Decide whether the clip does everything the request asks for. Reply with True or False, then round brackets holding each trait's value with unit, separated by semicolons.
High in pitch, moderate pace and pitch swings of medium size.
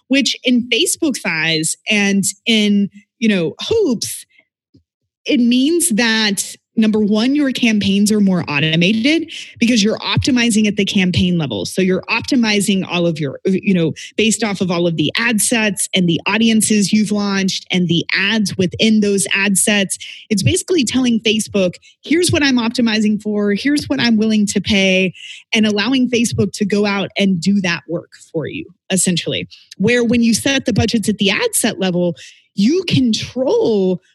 True (210 Hz; 165 wpm; 3.7 semitones)